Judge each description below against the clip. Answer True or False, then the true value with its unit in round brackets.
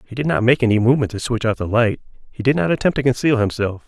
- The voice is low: True (120 Hz)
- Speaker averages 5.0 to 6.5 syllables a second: False (6.9 syllables/s)